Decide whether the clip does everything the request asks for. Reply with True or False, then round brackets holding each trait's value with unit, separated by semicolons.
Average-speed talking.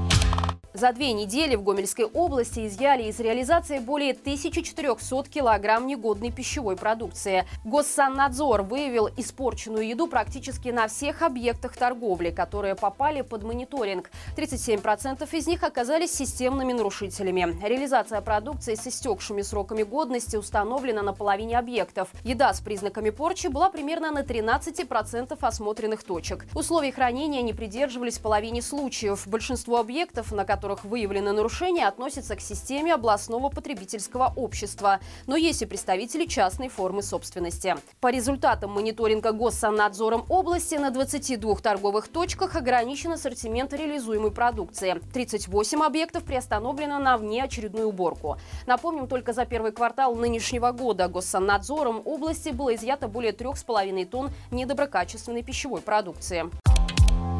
True (120 wpm)